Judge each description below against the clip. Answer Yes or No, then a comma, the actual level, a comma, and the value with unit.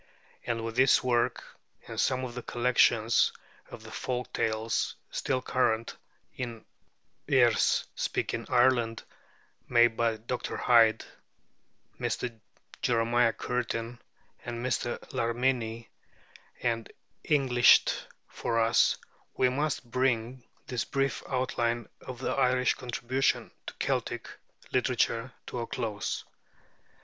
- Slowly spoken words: Yes, slow, 110 wpm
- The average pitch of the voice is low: Yes, low, 120 Hz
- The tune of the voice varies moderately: No, narrow, 1.7 semitones